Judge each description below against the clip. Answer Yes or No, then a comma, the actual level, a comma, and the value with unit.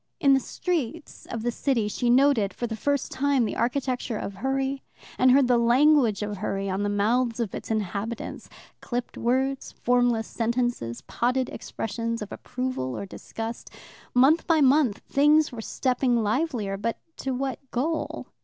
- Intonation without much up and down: No, average, 3.3 semitones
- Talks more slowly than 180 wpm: Yes, average, 160 wpm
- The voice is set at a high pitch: Yes, high, 245 Hz